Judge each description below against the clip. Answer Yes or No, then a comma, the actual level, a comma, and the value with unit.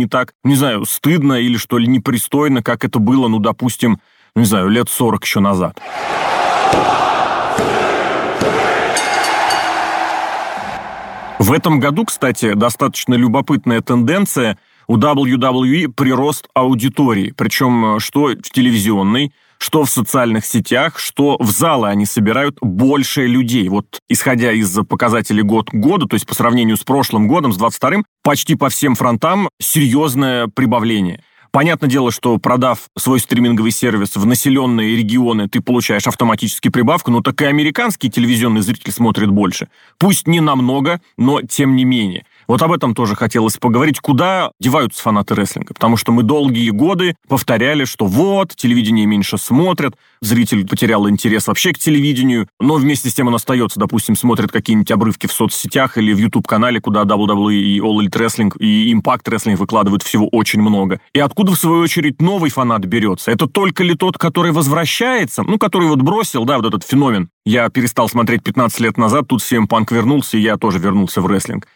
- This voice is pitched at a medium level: No, low, 125 Hz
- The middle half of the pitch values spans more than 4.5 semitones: Yes, average, 5.0 semitones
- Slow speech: No, fast, 160 wpm